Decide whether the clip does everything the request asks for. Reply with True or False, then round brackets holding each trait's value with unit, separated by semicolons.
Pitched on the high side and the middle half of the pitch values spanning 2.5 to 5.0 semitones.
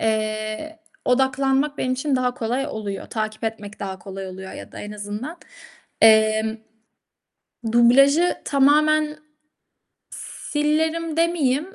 False (255 Hz; 5.6 semitones)